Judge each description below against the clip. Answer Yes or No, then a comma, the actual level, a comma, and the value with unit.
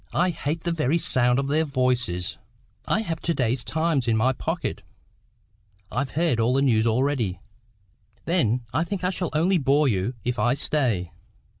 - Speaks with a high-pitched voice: No, low, 135 Hz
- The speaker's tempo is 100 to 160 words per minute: No, average, 175 wpm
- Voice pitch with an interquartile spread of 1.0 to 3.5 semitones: No, average, 5.1 semitones